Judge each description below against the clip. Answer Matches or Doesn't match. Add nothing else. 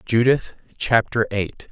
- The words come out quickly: Doesn't match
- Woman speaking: Doesn't match